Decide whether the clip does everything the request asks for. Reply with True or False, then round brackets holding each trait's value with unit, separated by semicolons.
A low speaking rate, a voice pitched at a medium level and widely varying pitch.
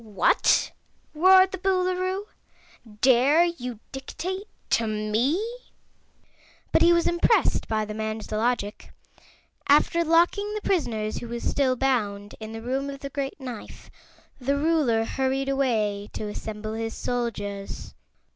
False (130 wpm; 260 Hz; 7.4 semitones)